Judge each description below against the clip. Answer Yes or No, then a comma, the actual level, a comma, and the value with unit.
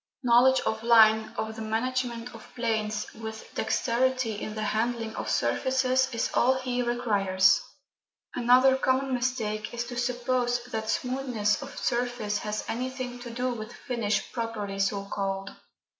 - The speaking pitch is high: Yes, high, 235 Hz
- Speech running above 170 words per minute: No, average, 145 wpm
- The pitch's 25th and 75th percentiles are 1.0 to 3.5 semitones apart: Yes, narrow, 2.5 semitones